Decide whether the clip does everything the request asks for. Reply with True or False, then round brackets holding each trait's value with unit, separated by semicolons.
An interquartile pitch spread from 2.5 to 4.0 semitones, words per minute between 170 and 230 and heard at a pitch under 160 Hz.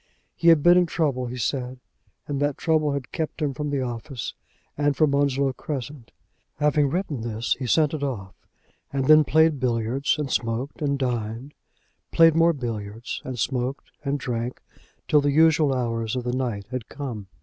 True (3.5 semitones; 175 wpm; 135 Hz)